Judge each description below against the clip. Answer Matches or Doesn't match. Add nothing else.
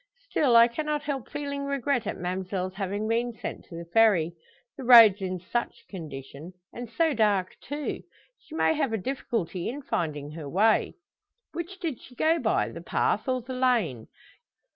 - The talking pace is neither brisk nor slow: Matches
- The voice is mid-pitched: Doesn't match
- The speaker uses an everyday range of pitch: Doesn't match